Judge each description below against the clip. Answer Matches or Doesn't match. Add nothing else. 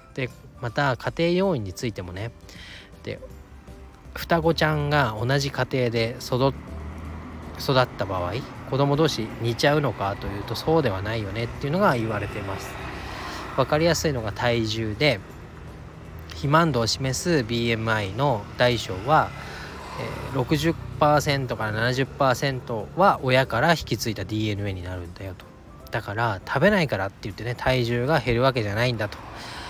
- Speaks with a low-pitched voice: Matches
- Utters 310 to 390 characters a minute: Doesn't match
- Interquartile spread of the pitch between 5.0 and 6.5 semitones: Matches